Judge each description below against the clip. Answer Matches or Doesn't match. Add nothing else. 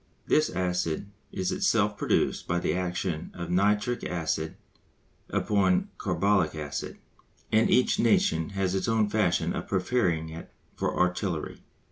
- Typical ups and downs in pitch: Matches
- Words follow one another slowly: Matches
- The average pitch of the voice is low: Matches